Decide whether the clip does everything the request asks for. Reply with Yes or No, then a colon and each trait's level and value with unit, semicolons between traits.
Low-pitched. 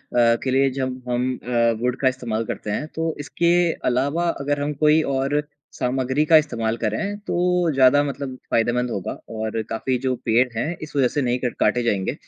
Yes: low, 130 Hz